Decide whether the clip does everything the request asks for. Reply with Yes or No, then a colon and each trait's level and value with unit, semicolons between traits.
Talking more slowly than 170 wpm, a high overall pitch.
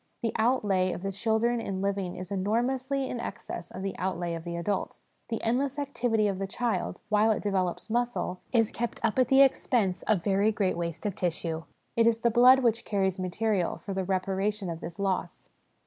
No: average, 195 wpm; high, 205 Hz